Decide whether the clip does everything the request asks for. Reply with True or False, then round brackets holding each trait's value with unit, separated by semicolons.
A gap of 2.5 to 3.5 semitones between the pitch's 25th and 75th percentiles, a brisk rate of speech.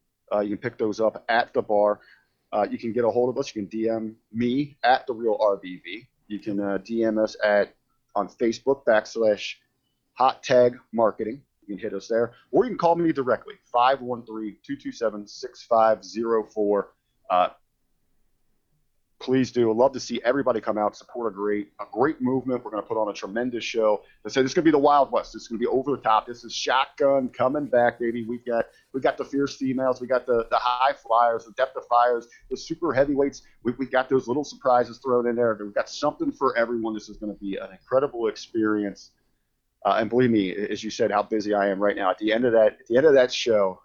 True (3.2 semitones; 220 wpm)